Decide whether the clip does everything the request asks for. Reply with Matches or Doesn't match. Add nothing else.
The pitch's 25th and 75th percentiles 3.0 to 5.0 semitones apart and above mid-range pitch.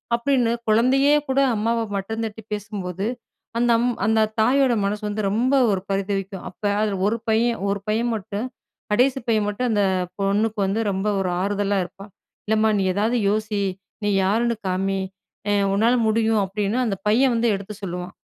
Doesn't match